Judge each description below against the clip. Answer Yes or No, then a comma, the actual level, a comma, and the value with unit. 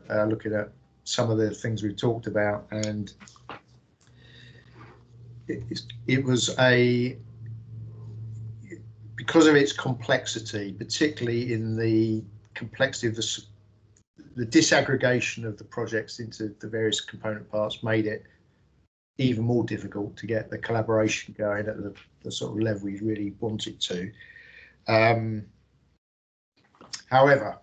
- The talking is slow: Yes, slow, 125 wpm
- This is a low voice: Yes, low, 110 Hz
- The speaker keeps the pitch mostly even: Yes, narrow, 1.9 semitones